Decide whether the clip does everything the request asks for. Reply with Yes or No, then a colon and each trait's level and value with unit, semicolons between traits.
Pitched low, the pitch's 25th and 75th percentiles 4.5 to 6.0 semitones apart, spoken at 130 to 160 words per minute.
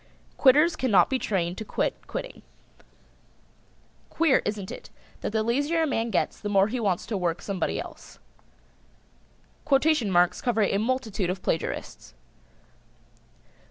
No: high, 220 Hz; wide, 5.6 semitones; average, 140 wpm